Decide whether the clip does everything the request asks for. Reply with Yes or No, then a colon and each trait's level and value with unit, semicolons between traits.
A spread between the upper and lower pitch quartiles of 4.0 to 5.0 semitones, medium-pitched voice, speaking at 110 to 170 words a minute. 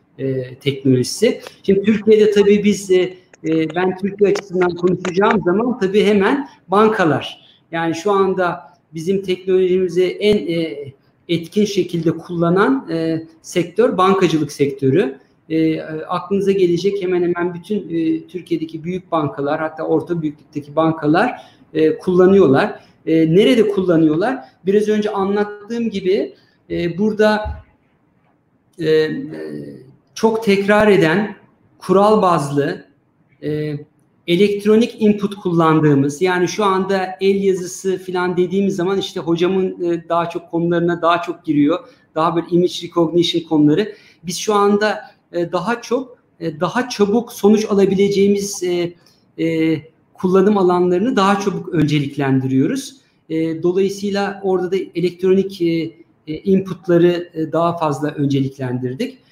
No: average, 3.6 semitones; medium, 180 Hz; average, 115 wpm